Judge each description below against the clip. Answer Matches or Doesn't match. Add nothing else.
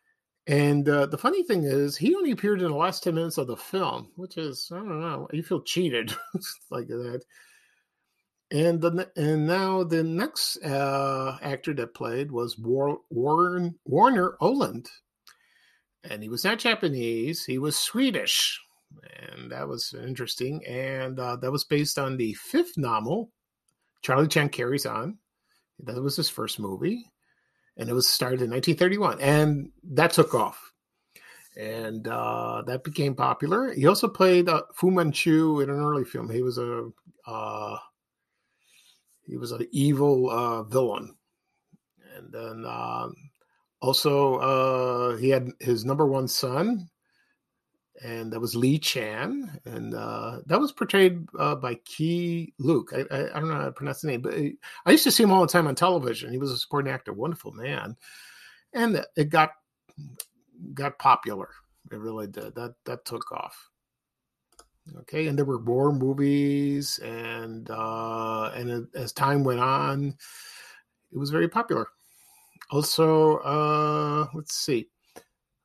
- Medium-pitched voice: Matches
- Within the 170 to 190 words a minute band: Doesn't match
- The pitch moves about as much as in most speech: Matches